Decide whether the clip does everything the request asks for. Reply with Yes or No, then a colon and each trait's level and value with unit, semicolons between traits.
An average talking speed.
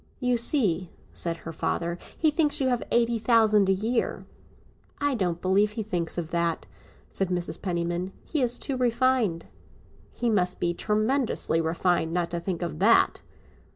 Yes: average, 160 wpm